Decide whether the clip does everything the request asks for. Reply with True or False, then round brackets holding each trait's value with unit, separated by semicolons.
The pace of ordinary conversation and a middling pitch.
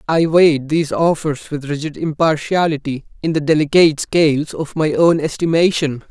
True (145 wpm; 155 Hz)